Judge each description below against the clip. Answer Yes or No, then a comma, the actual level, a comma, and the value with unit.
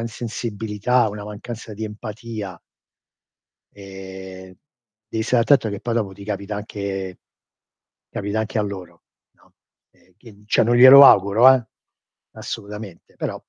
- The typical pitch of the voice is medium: No, low, 105 Hz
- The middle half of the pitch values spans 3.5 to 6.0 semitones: No, average, 2.7 semitones